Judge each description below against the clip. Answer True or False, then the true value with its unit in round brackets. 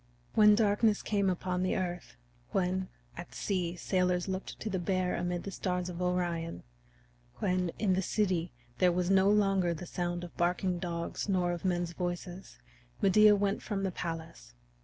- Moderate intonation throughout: False (1.8 semitones)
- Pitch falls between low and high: True (180 Hz)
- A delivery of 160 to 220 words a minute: True (165 wpm)